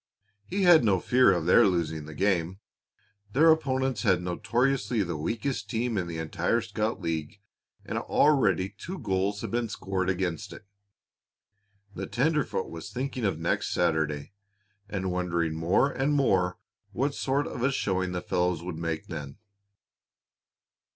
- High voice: No, very low, 95 Hz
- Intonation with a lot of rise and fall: Yes, wide, 6.3 semitones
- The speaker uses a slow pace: No, average, 150 wpm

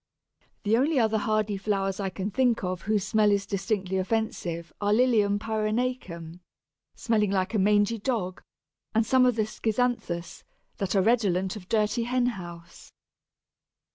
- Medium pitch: No, high, 210 Hz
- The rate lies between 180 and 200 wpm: No, average, 145 wpm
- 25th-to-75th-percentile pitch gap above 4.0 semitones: No, average, 3.0 semitones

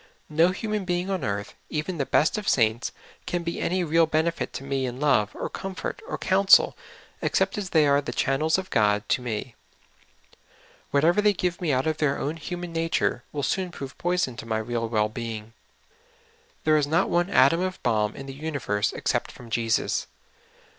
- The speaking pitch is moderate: Yes, medium, 150 Hz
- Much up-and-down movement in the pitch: Yes, wide, 6.6 semitones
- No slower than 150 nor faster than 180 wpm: No, average, 190 wpm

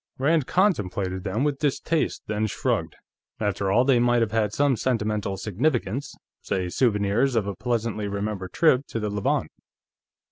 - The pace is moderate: Yes, average, 150 wpm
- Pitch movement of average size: Yes, average, 4.4 semitones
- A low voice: Yes, low, 110 Hz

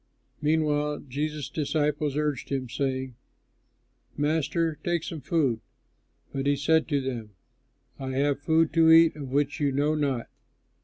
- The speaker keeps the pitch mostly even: Yes, narrow, 2.3 semitones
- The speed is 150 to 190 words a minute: No, average, 140 wpm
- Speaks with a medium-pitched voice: Yes, medium, 145 Hz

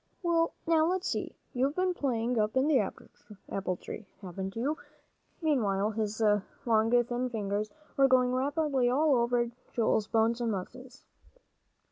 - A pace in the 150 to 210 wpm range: No, average, 140 wpm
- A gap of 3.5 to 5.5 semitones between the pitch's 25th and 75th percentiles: Yes, average, 4.1 semitones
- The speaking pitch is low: No, high, 245 Hz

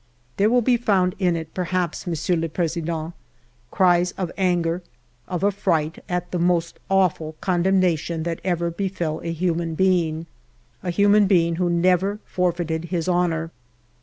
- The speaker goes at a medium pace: Yes, average, 155 wpm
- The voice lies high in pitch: No, medium, 175 Hz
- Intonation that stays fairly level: Yes, narrow, 2.0 semitones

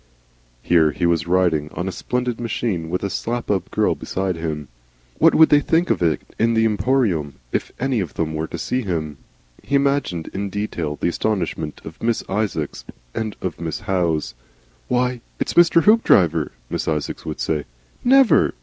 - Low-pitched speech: Yes, very low, 95 Hz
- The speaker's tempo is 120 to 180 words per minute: Yes, average, 175 wpm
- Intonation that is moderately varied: No, wide, 6.8 semitones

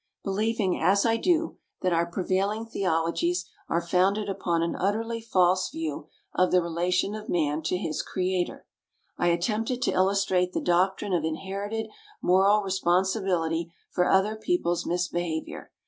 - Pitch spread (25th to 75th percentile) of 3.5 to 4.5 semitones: No, average, 3.0 semitones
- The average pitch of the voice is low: No, medium, 185 Hz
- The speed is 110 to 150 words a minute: Yes, average, 140 wpm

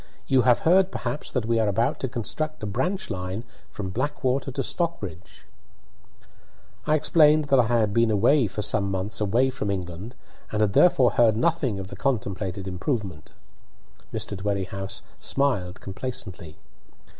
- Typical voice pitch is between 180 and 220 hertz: No, low, 115 Hz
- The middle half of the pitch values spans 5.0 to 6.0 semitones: Yes, wide, 5.5 semitones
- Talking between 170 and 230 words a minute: No, average, 145 wpm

